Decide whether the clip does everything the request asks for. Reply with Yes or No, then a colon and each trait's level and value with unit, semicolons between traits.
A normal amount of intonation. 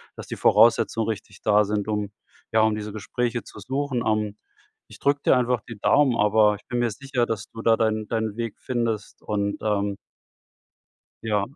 No: narrow, 2.1 semitones